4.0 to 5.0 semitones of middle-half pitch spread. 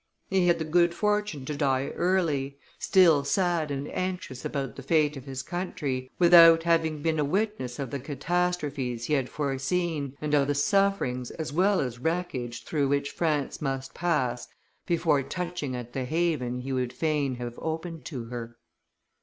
Yes: average, 4.5 semitones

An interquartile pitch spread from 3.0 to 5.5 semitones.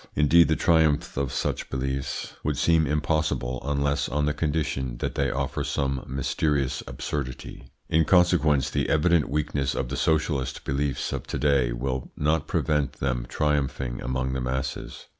No: narrow, 2.5 semitones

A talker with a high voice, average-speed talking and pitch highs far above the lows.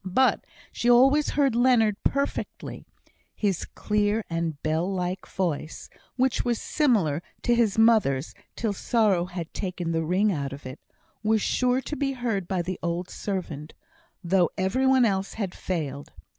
Yes: high, 195 Hz; average, 155 wpm; wide, 5.7 semitones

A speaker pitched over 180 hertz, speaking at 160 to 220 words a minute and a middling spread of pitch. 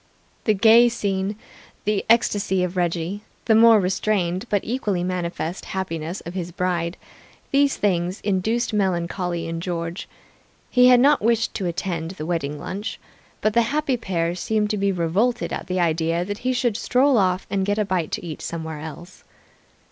Yes: high, 190 Hz; average, 170 wpm; average, 4.2 semitones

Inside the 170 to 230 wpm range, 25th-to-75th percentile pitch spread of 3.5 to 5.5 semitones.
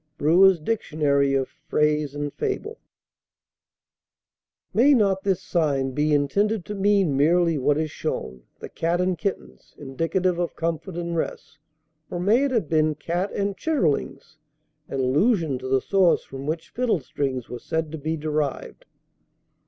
No: average, 145 wpm; average, 5.0 semitones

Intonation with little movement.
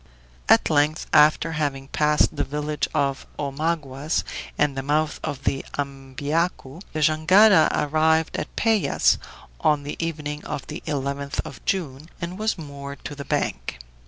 Yes: narrow, 2.3 semitones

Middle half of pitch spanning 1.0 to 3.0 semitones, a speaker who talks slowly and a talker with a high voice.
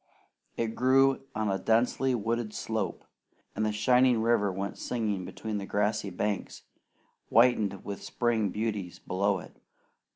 No: average, 2.7 semitones; slow, 130 wpm; low, 110 Hz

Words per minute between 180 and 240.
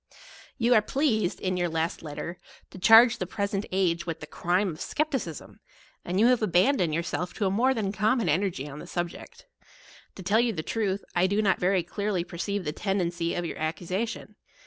Yes: average, 200 wpm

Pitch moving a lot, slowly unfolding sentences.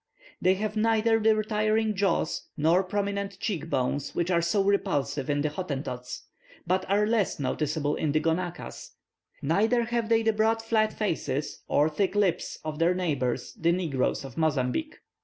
No: wide, 6.0 semitones; average, 160 wpm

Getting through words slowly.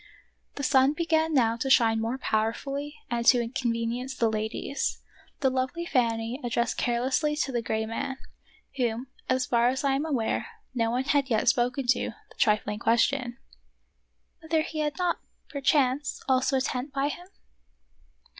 No: average, 165 wpm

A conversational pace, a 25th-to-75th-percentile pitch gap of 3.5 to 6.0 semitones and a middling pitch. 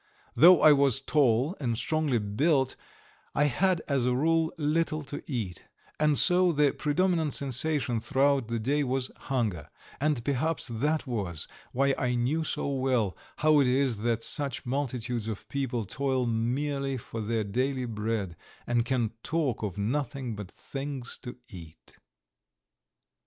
No: average, 145 wpm; average, 4.1 semitones; low, 130 Hz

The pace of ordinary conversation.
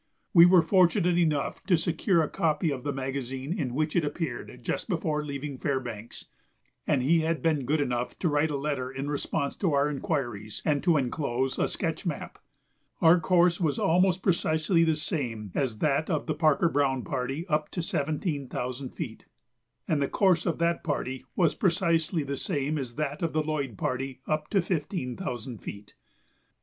Yes: average, 180 wpm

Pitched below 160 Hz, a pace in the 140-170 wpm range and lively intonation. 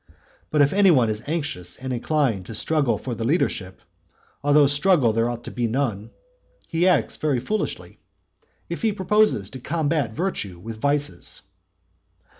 Yes: medium, 140 Hz; average, 155 wpm; wide, 5.8 semitones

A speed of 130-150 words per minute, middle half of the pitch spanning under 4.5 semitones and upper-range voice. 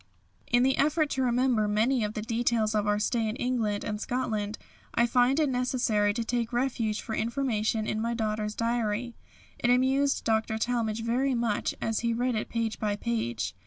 No: average, 185 wpm; narrow, 2.4 semitones; high, 230 Hz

